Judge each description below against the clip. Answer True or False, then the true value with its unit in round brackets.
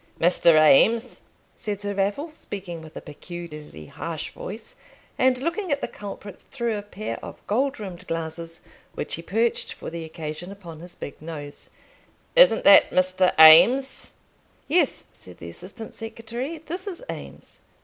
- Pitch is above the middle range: True (195 Hz)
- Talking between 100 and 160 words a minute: True (150 wpm)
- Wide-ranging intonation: True (7.1 semitones)